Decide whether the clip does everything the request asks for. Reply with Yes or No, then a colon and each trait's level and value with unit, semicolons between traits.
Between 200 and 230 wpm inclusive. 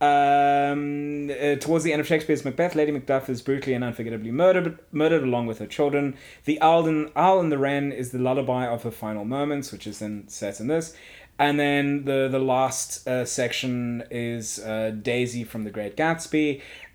No: average, 190 wpm